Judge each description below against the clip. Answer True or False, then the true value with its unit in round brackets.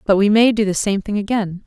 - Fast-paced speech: True (290 wpm)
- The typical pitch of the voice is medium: False (205 Hz)